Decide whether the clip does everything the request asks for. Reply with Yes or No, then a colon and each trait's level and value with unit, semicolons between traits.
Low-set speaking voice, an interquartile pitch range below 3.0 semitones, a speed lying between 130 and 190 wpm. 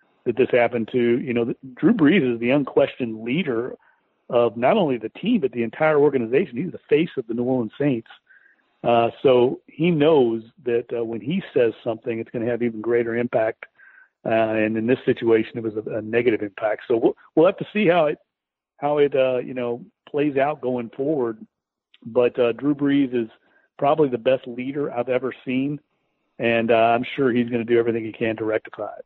No: low, 120 Hz; narrow, 2.4 semitones; fast, 205 wpm